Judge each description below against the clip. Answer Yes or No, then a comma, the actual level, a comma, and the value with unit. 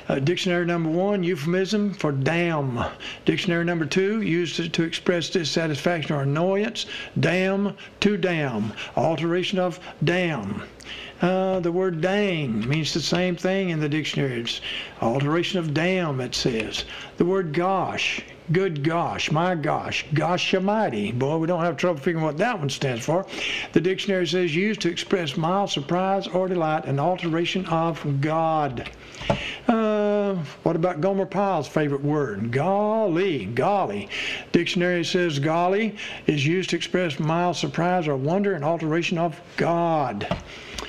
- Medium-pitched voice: Yes, medium, 170 Hz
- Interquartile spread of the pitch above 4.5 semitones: No, average, 3.2 semitones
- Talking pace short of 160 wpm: Yes, average, 145 wpm